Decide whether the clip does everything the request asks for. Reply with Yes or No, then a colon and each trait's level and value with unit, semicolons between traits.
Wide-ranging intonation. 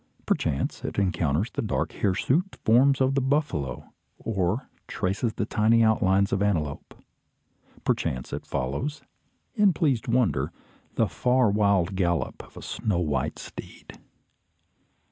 Yes: wide, 6.5 semitones